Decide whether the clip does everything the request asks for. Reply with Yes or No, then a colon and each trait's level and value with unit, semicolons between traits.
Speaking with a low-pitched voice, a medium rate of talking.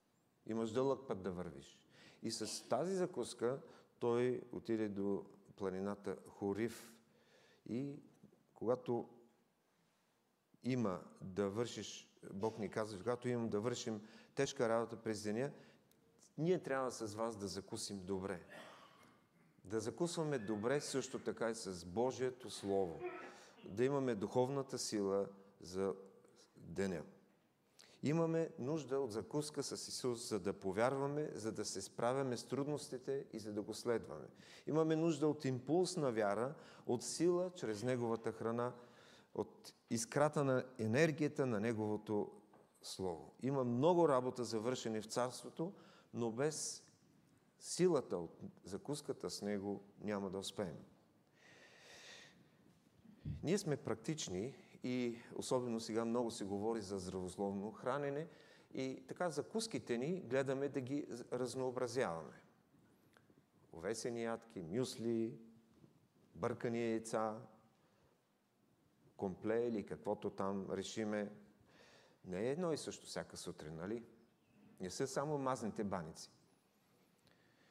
No: low, 120 Hz; slow, 115 wpm